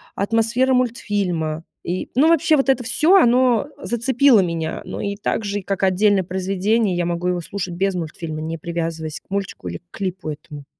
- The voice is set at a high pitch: Yes, high, 195 Hz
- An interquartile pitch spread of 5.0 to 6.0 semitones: Yes, average, 5.3 semitones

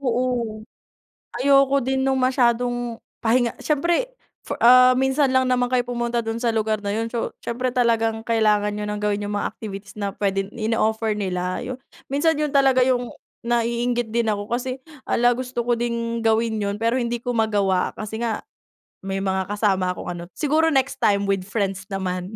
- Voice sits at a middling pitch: No, high, 230 Hz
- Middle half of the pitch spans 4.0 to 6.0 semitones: No, average, 3.3 semitones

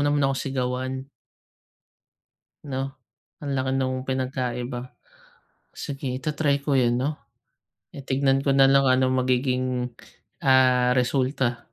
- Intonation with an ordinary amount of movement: No, narrow, 1.3 semitones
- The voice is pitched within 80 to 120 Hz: No, low, 130 Hz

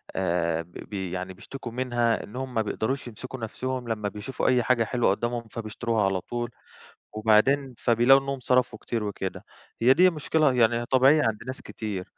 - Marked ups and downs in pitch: No, average, 3.4 semitones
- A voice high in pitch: No, low, 120 Hz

